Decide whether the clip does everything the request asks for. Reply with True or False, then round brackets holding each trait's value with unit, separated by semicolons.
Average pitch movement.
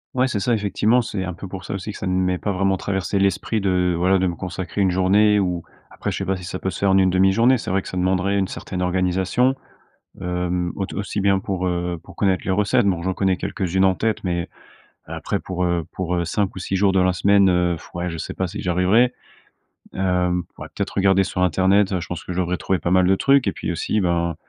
False (1.6 semitones)